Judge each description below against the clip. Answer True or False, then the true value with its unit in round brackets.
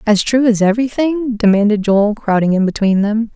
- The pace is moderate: True (180 wpm)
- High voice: True (220 Hz)